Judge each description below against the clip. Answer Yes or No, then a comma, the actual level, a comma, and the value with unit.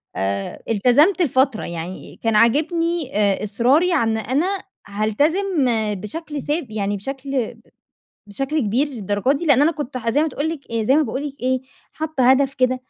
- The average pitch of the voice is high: Yes, very high, 260 Hz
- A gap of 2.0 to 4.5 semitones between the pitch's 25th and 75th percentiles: No, wide, 5.5 semitones